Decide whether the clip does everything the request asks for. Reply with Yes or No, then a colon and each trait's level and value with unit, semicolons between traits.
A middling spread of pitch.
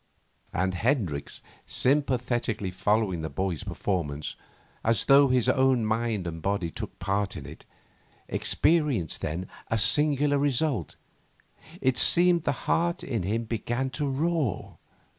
No: wide, 6.7 semitones